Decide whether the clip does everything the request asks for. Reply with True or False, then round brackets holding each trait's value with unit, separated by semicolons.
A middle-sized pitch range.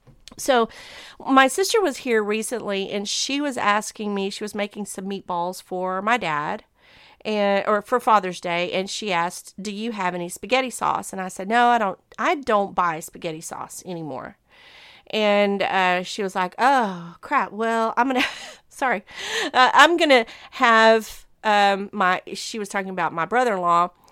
True (4.2 semitones)